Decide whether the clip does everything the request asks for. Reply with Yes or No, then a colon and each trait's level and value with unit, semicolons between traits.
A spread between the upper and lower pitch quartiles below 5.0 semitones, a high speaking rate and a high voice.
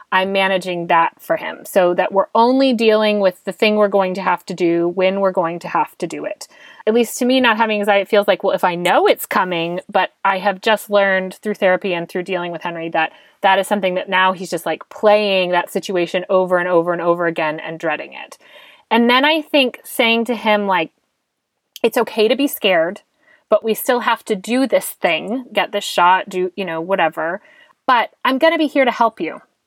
Yes: average, 4.0 semitones; fast, 230 wpm; high, 195 Hz